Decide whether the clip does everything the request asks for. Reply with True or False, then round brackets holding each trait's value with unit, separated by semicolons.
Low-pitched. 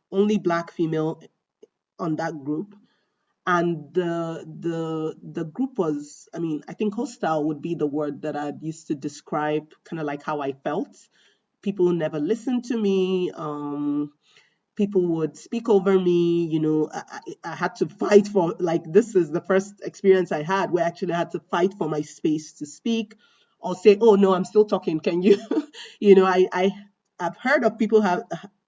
False (175 Hz)